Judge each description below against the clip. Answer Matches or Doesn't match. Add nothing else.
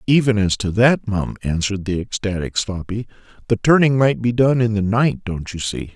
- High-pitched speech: Doesn't match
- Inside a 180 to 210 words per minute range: Matches